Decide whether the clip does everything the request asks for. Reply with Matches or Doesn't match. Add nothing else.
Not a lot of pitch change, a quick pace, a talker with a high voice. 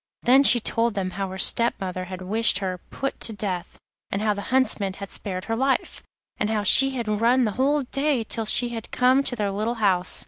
Doesn't match